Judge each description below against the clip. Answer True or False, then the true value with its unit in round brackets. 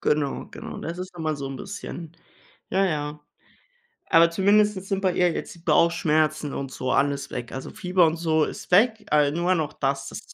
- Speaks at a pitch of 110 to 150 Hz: False (160 Hz)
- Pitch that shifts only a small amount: False (3.8 semitones)